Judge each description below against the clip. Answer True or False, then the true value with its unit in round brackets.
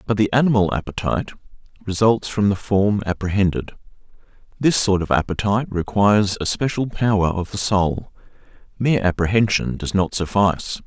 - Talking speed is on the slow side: True (130 wpm)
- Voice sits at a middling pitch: False (100 Hz)